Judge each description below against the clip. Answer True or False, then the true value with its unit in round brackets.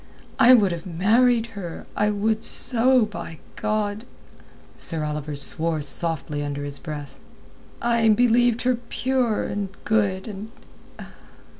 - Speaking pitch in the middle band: False (205 Hz)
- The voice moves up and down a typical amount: False (6.0 semitones)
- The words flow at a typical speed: False (125 wpm)